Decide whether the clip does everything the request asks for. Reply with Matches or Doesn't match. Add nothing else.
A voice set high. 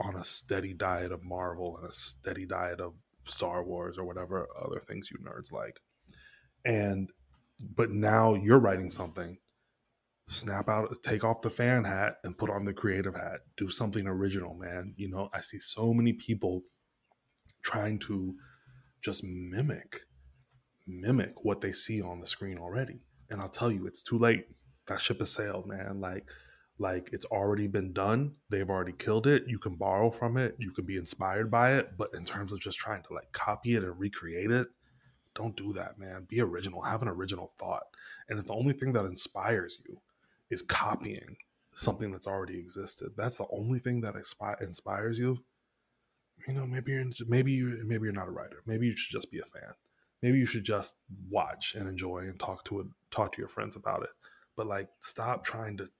Doesn't match